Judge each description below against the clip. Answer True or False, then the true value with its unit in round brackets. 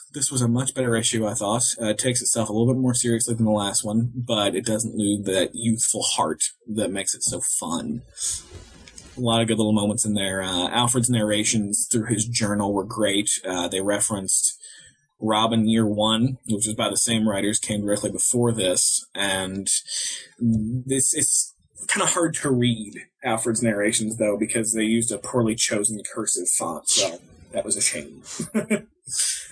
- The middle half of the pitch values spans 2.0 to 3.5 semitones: True (2.6 semitones)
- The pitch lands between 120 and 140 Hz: False (110 Hz)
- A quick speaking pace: False (180 wpm)